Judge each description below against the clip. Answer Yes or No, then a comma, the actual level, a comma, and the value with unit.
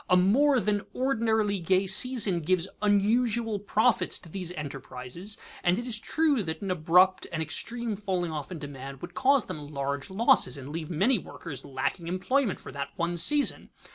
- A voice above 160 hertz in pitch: Yes, medium, 185 Hz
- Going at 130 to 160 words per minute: No, average, 170 wpm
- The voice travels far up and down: Yes, wide, 5.7 semitones